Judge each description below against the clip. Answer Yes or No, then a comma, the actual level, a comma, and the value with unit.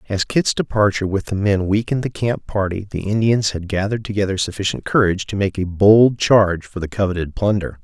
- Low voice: Yes, low, 100 Hz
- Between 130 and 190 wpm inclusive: No, average, 200 wpm